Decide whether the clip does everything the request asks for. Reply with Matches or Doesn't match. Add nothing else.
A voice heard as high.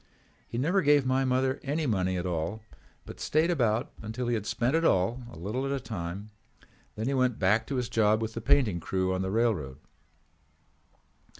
Doesn't match